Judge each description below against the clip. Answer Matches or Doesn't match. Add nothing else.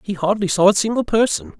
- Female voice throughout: Doesn't match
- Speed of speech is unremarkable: Doesn't match